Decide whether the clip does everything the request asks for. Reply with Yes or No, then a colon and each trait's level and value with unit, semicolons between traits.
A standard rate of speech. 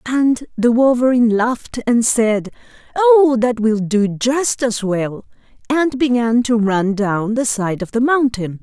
Yes: average, 160 wpm